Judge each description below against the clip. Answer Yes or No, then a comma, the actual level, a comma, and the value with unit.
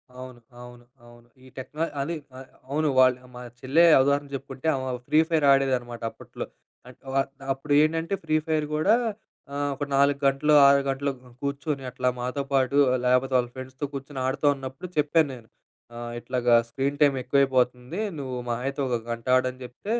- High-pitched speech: No, low, 135 Hz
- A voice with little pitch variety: Yes, narrow, 2.1 semitones